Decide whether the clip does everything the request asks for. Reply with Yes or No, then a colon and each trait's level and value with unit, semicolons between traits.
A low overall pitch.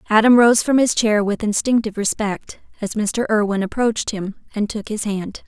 No: high, 215 Hz